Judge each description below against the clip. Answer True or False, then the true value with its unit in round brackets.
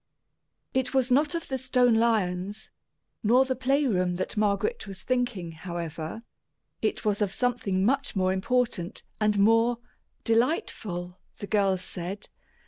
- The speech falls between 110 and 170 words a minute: True (135 wpm)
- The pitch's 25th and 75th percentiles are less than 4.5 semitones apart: False (5.0 semitones)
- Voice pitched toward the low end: False (215 Hz)